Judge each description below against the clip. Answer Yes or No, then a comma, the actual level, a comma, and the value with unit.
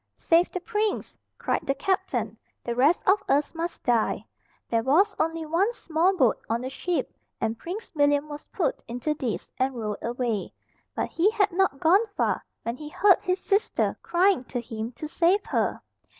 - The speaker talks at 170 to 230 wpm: Yes, average, 180 wpm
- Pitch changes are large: Yes, wide, 7.0 semitones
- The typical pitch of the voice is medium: No, very high, 315 Hz